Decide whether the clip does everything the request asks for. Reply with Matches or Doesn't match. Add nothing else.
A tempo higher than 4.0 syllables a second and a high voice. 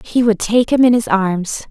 Matches